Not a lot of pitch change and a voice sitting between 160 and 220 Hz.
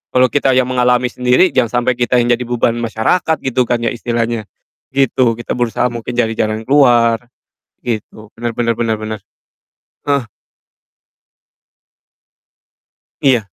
No: narrow, 1.7 semitones; low, 120 Hz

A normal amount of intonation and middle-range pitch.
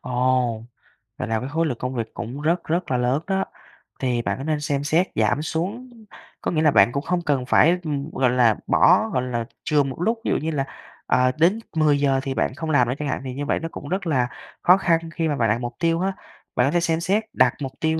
Yes: average, 4.6 semitones; medium, 145 Hz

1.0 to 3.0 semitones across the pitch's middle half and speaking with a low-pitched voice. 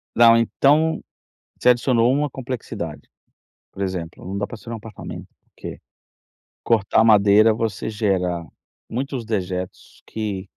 No: average, 3.5 semitones; low, 110 Hz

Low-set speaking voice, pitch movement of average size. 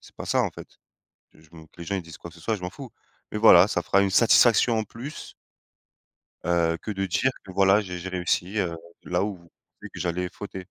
Yes: very low, 95 Hz; average, 3.4 semitones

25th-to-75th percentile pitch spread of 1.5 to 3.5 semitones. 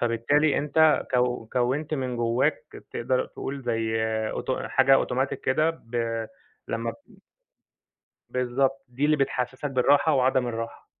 Yes: average, 2.8 semitones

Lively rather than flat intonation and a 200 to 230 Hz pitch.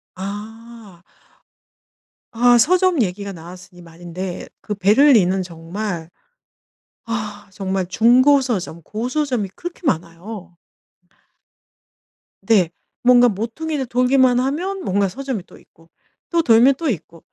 Yes: wide, 5.7 semitones; high, 215 Hz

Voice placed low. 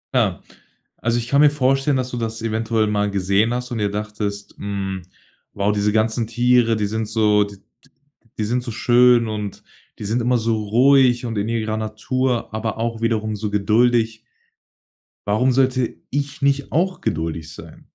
Yes: low, 115 Hz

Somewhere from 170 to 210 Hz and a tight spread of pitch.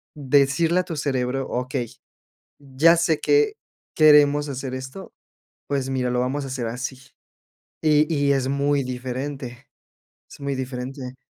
No: low, 135 Hz; narrow, 2.2 semitones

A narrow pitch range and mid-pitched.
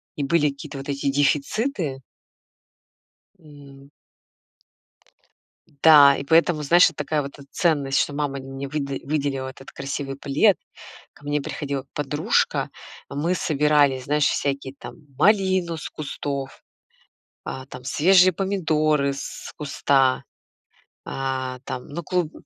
Yes: narrow, 2.3 semitones; medium, 145 Hz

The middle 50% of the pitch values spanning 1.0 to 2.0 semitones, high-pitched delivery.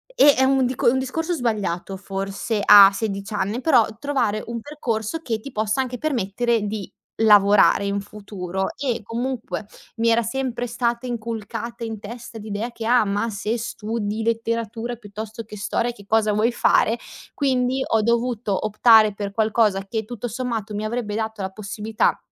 No: narrow, 2.6 semitones; high, 225 Hz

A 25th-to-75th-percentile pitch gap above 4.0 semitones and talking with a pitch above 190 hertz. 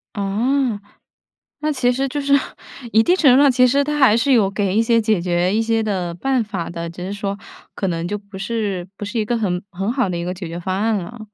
Yes: average, 4.8 semitones; high, 210 Hz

